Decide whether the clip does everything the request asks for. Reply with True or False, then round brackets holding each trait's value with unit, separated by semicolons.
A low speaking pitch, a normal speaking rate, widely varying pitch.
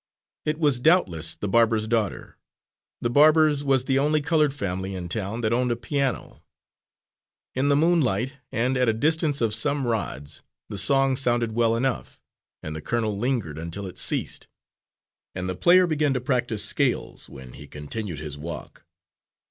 True (120 Hz; 165 wpm; 6.3 semitones)